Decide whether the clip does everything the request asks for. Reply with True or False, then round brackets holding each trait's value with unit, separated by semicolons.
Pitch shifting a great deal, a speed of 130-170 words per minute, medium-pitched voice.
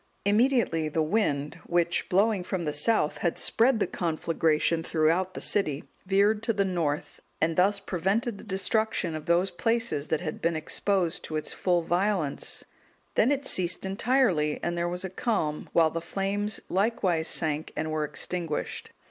False (4.3 semitones; 165 wpm; 175 Hz)